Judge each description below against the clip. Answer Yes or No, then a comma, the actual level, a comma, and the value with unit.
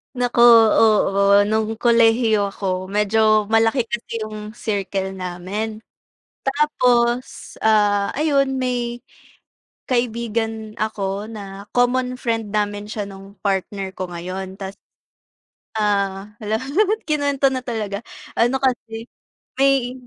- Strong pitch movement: No, average, 3.2 semitones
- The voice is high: Yes, high, 215 Hz